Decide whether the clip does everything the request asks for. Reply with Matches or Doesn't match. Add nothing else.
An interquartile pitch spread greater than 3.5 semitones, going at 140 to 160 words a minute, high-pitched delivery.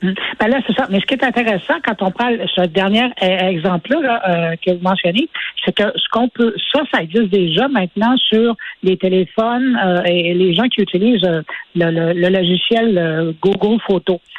Doesn't match